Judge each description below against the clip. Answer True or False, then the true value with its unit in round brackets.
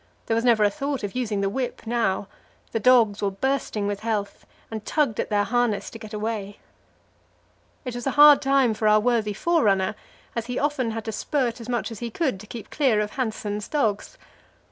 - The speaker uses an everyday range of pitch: True (3.4 semitones)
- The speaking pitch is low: False (225 Hz)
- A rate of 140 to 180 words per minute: False (200 wpm)